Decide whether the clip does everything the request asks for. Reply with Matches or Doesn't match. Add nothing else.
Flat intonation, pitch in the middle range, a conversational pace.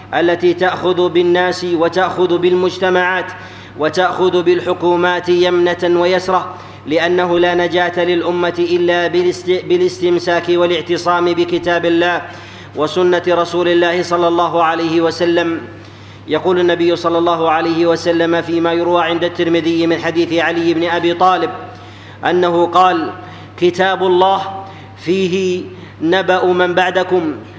Matches